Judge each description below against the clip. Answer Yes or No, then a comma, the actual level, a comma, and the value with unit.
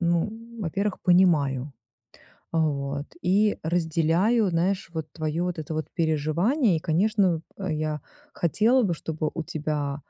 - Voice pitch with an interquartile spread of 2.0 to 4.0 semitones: Yes, average, 3.4 semitones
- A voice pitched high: No, medium, 165 Hz